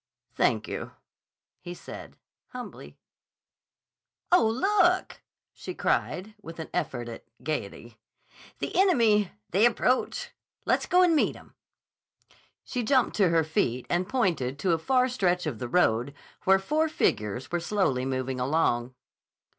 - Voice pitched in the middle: Yes, medium, 180 Hz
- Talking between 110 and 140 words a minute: Yes, slow, 135 wpm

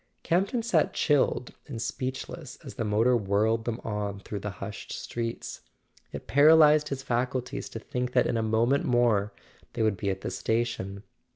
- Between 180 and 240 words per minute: No, average, 170 wpm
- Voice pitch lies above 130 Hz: No, low, 115 Hz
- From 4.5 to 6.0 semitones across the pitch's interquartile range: No, average, 3.9 semitones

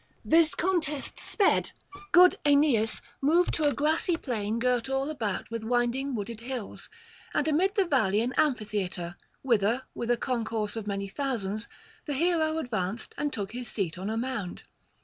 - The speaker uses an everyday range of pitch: No, wide, 5.7 semitones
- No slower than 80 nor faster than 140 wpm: No, average, 160 wpm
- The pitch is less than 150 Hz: No, high, 245 Hz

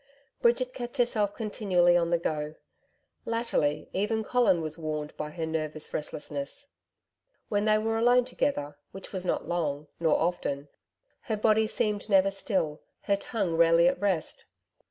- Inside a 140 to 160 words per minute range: Yes, average, 150 wpm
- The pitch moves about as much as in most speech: No, wide, 5.7 semitones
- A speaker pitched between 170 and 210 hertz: Yes, medium, 185 Hz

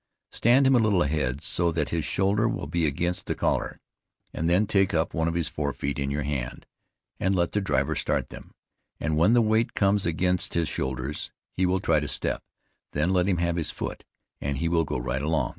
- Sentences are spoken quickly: Yes, fast, 220 wpm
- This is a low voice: Yes, very low, 85 Hz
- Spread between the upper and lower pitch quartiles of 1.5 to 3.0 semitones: No, average, 4.2 semitones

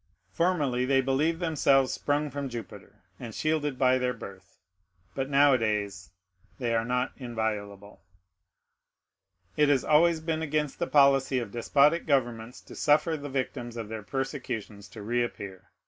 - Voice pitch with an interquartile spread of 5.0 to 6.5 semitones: No, average, 4.3 semitones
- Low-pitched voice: Yes, low, 130 Hz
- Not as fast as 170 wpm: Yes, average, 140 wpm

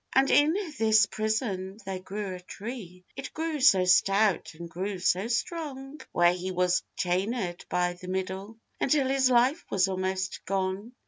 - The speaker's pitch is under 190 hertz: No, high, 195 Hz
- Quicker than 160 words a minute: No, average, 155 wpm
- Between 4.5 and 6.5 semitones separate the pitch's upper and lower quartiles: Yes, average, 5.1 semitones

